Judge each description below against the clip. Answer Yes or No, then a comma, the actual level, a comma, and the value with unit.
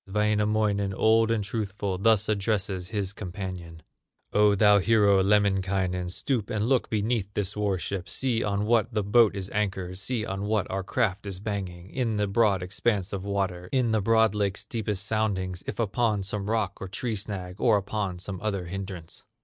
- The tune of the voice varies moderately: No, narrow, 2.1 semitones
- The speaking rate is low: No, average, 175 wpm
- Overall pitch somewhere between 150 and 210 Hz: No, low, 100 Hz